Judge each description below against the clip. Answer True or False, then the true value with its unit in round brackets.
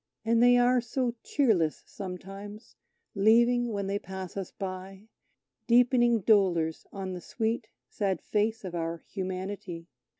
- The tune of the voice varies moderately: True (3.9 semitones)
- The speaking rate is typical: False (130 wpm)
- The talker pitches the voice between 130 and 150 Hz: False (200 Hz)